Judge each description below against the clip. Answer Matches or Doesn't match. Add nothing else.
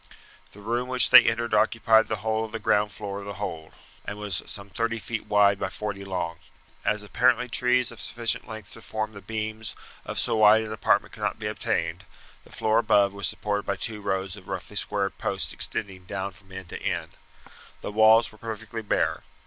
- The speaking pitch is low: Matches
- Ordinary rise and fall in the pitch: Doesn't match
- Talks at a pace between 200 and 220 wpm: Matches